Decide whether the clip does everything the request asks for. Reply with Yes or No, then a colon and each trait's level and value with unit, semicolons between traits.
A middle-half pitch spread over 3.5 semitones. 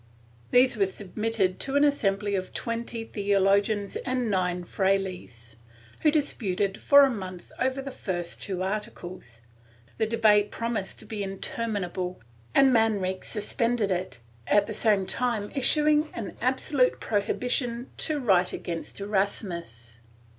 Yes: average, 4.1 semitones